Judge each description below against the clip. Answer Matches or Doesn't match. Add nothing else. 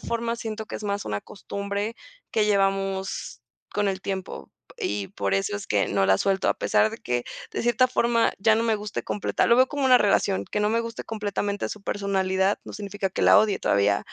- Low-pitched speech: Doesn't match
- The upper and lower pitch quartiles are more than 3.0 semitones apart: Doesn't match